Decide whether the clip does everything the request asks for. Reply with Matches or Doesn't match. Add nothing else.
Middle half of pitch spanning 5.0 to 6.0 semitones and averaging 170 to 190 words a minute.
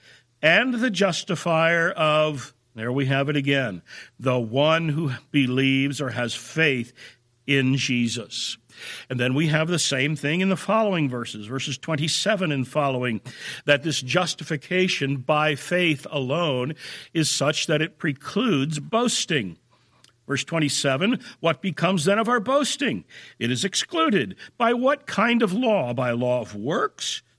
Doesn't match